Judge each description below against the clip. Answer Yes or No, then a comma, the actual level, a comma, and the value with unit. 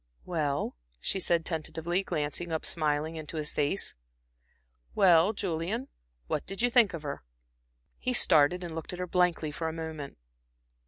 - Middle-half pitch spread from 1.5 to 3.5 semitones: Yes, average, 2.8 semitones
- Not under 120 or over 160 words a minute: Yes, average, 155 wpm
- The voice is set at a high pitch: No, medium, 165 Hz